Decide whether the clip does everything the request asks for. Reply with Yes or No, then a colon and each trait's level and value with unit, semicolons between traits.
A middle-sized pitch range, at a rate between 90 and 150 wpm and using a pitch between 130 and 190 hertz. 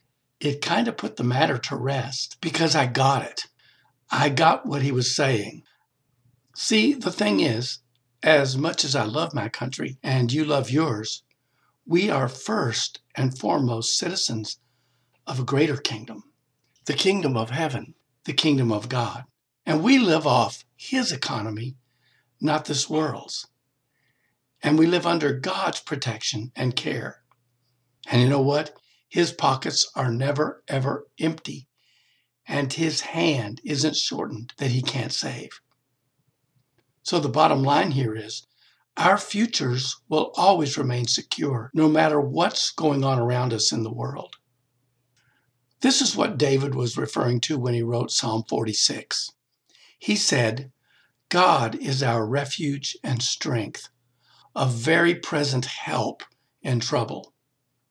Yes: average, 3.7 semitones; average, 140 wpm; low, 135 Hz